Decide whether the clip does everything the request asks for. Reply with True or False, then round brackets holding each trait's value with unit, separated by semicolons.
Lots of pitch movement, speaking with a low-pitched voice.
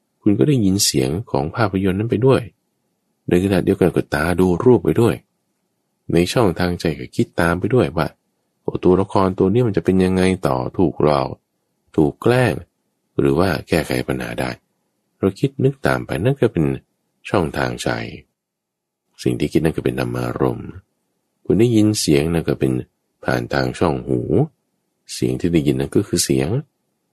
True (6.7 semitones; 85 Hz)